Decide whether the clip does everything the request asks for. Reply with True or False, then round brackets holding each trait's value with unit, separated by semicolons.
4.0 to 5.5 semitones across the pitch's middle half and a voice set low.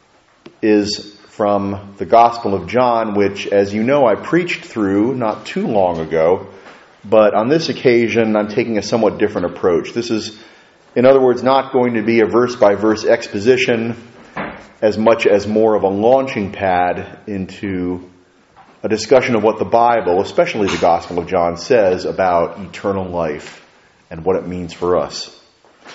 False (2.9 semitones; 110 Hz)